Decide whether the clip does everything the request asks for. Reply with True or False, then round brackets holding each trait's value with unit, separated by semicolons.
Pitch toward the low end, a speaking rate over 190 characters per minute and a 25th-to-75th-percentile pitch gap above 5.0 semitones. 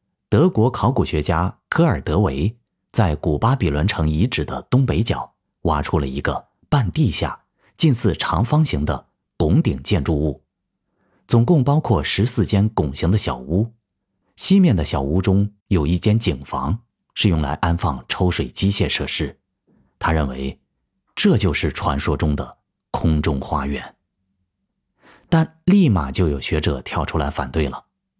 True (95 Hz; 215 characters per minute; 5.5 semitones)